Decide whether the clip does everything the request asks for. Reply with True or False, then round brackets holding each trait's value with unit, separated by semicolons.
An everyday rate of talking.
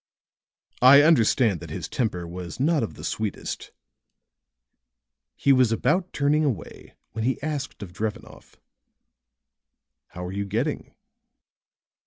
False (120 wpm)